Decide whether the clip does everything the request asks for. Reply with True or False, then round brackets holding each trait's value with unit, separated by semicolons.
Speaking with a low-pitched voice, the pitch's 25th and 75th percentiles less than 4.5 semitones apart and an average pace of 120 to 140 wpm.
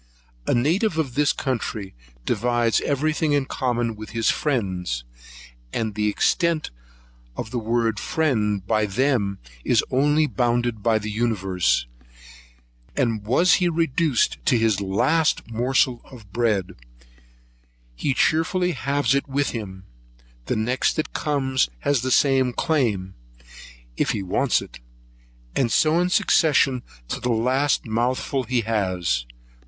False (120 Hz; 4.9 semitones; 135 wpm)